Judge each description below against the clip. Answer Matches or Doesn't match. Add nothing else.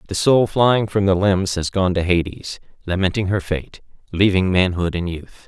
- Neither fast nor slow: Matches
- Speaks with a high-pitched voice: Doesn't match